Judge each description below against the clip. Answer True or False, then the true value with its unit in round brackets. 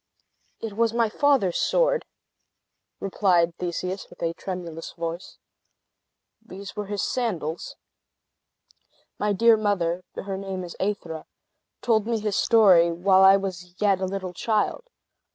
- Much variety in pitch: False (3.2 semitones)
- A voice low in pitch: False (195 Hz)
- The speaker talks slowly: True (130 wpm)